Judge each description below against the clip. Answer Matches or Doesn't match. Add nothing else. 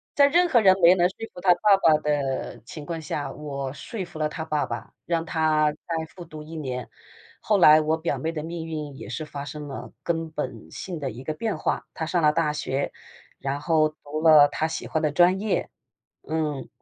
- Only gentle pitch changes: Matches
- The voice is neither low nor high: Matches